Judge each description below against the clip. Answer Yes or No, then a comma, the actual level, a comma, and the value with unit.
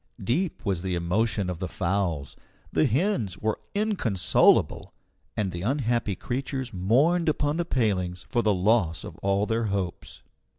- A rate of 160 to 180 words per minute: No, average, 145 wpm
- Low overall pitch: Yes, low, 105 Hz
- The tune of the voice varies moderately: No, wide, 6.1 semitones